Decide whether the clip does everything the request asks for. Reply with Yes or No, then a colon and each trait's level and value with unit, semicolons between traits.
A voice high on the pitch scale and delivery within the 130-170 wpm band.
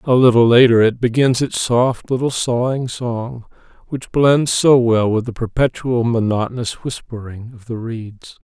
No: low, 120 Hz; average, 155 wpm